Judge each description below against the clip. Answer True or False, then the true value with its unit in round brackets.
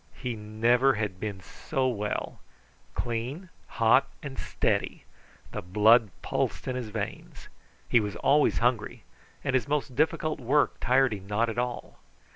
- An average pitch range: True (3.8 semitones)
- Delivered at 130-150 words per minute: True (145 wpm)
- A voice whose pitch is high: False (120 Hz)